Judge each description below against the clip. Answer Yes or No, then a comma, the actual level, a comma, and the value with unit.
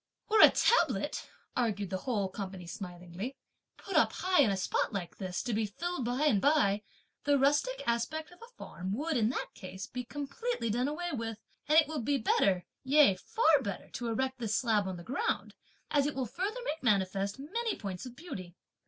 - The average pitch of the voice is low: No, high, 245 Hz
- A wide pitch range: Yes, wide, 7.0 semitones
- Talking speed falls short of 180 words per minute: No, average, 200 wpm